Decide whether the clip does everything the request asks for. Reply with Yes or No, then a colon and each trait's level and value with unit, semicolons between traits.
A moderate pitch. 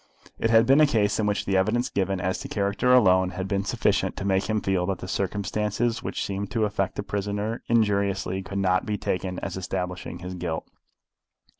No: low, 100 Hz